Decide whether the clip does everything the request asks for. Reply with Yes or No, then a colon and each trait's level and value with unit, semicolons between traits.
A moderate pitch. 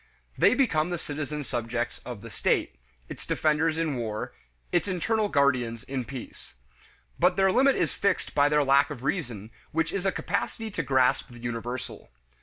Yes: medium, 145 Hz